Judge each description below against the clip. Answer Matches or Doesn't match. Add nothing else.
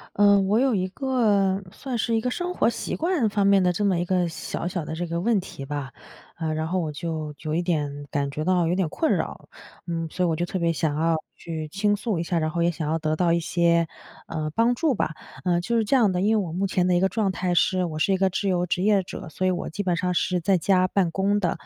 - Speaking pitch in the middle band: Matches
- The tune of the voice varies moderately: Matches